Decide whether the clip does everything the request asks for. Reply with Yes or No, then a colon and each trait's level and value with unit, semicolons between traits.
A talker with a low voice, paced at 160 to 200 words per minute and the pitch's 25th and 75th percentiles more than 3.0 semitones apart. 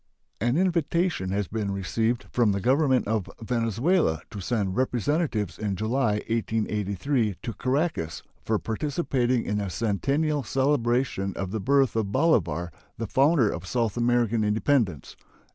No: low, 115 Hz; slow, 135 wpm; average, 4.9 semitones